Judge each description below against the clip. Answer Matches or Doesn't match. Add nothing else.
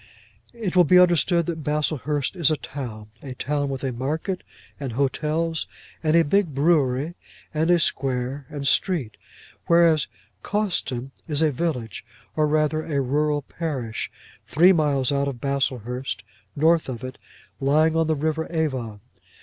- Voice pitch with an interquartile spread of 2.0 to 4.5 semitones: Matches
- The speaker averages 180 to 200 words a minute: Doesn't match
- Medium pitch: Matches